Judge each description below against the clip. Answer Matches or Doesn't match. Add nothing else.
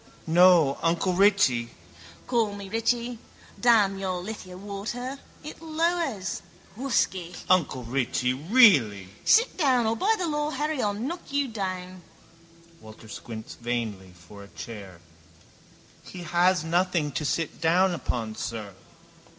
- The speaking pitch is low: Doesn't match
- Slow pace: Matches